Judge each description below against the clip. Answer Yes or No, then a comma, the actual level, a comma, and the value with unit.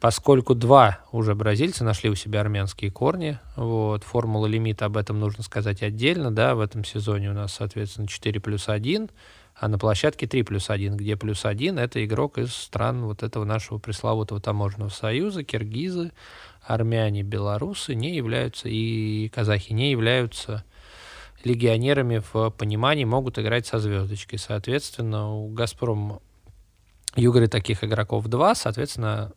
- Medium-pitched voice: No, low, 110 Hz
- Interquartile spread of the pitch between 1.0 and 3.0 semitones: Yes, narrow, 2.5 semitones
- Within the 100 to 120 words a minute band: No, average, 145 wpm